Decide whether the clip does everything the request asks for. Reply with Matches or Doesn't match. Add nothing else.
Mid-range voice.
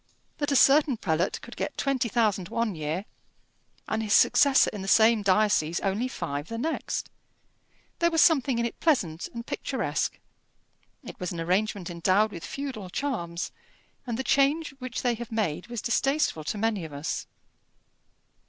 Doesn't match